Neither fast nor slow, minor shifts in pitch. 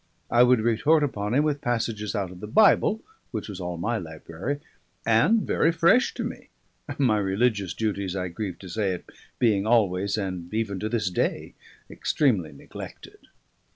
No: average, 165 wpm; average, 4.3 semitones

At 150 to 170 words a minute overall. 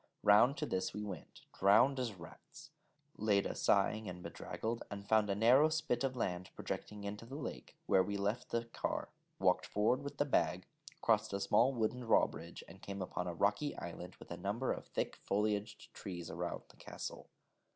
No: average, 185 wpm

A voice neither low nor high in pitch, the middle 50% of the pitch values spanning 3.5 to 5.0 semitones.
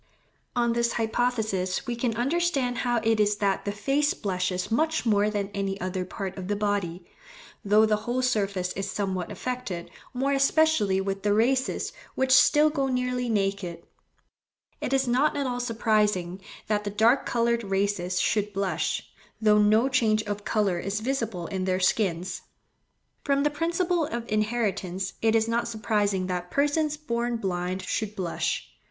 No: high, 215 Hz; average, 4.1 semitones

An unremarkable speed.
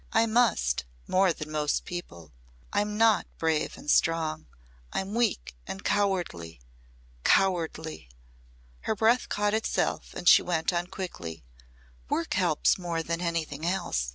No: slow, 130 wpm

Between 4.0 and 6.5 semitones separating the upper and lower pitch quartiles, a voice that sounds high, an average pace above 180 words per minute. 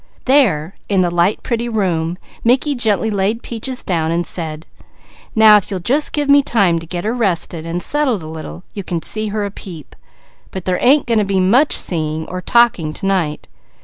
Yes: wide, 5.5 semitones; high, 195 Hz; average, 200 wpm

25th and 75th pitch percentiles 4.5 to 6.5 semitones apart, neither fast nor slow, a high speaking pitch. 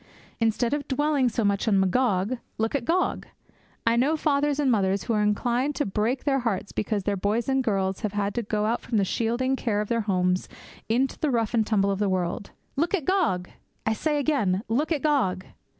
No: average, 5.0 semitones; fast, 215 wpm; high, 230 Hz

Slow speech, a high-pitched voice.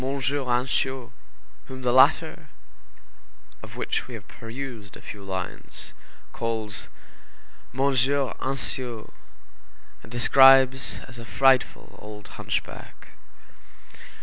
No: slow, 95 wpm; low, 125 Hz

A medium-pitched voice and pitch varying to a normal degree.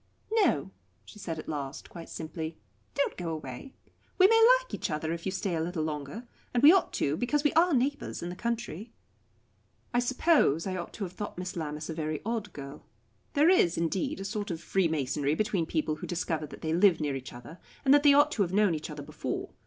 No: medium, 175 Hz; wide, 7.3 semitones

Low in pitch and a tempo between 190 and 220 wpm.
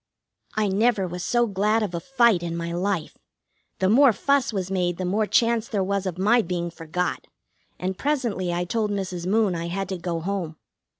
No: high, 190 Hz; average, 195 wpm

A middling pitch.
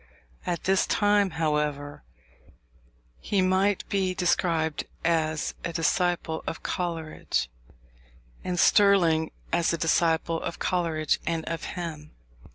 Yes: medium, 165 Hz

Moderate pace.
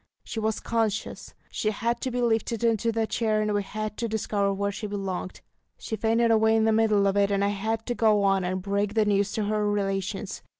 No: fast, 225 wpm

